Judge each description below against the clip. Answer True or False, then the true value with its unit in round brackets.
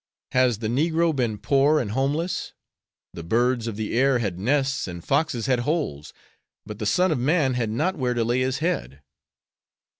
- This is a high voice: False (125 Hz)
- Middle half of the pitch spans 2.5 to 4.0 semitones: False (4.8 semitones)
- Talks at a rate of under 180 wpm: False (185 wpm)